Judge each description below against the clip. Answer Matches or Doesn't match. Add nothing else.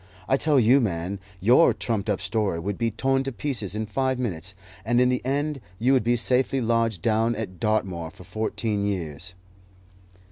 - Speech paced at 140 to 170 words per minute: Doesn't match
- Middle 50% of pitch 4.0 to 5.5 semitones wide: Matches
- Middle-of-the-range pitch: Doesn't match